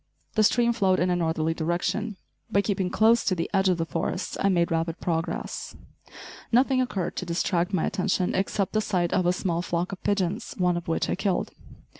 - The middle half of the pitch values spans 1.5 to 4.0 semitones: Yes, average, 2.8 semitones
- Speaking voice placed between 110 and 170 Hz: No, medium, 185 Hz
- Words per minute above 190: Yes, average, 200 wpm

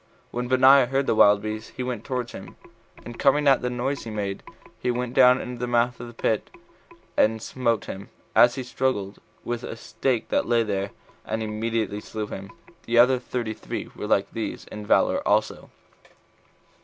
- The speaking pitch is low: Yes, low, 120 Hz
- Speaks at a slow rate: No, average, 185 wpm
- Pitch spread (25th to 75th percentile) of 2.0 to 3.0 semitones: Yes, narrow, 2.6 semitones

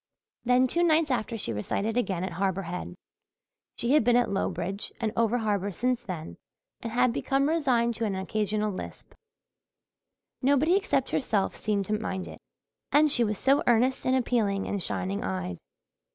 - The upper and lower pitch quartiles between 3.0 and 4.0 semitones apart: No, average, 4.6 semitones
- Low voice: No, high, 225 Hz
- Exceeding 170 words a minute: No, average, 165 wpm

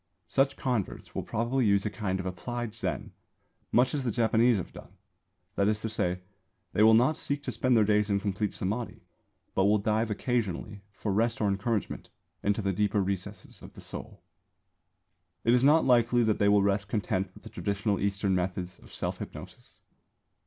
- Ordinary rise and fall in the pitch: Yes, average, 3.0 semitones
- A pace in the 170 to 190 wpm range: Yes, average, 185 wpm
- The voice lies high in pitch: No, low, 105 Hz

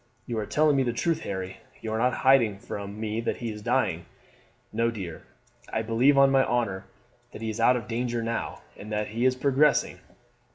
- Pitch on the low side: Yes, low, 115 Hz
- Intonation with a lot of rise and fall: No, average, 3.2 semitones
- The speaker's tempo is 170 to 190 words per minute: No, fast, 205 wpm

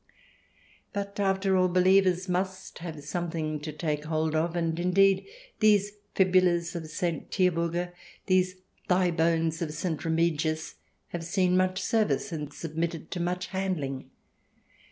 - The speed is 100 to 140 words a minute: Yes, slow, 135 wpm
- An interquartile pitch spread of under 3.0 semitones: Yes, narrow, 2.5 semitones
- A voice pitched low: No, medium, 175 Hz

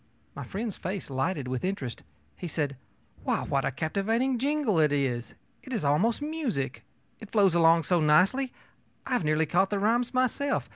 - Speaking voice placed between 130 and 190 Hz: Yes, medium, 185 Hz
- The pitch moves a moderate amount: No, wide, 8.0 semitones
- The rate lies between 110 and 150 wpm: No, average, 175 wpm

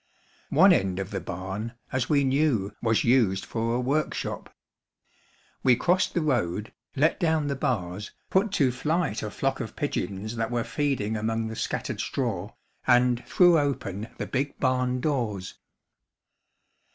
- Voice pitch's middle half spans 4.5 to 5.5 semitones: Yes, average, 4.9 semitones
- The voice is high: No, low, 125 Hz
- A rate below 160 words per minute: Yes, average, 150 wpm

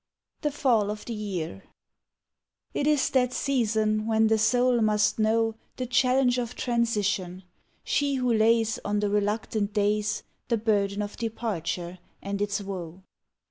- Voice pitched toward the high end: Yes, high, 215 Hz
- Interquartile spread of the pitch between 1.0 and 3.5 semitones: Yes, narrow, 2.6 semitones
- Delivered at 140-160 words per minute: Yes, average, 145 wpm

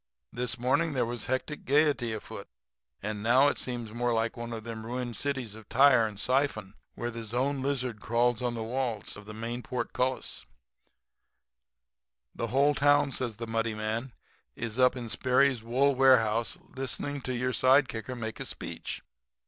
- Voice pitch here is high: No, low, 120 Hz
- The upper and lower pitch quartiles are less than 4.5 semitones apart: Yes, narrow, 2.6 semitones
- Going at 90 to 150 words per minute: No, average, 175 wpm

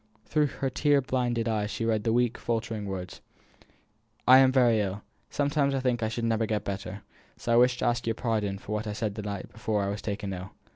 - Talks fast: Yes, fast, 230 wpm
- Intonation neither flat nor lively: Yes, average, 3.1 semitones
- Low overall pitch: Yes, low, 115 Hz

